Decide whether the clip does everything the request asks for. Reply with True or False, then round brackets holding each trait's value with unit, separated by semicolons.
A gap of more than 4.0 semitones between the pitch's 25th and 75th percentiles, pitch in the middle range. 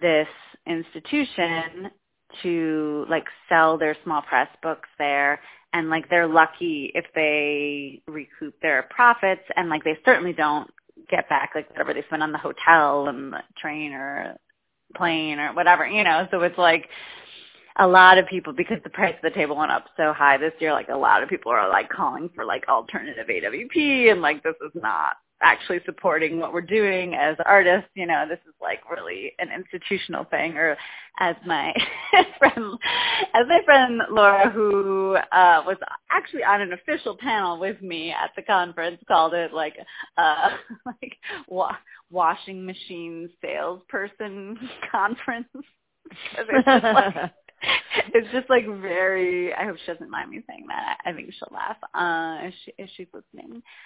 True (5.0 semitones; 180 Hz)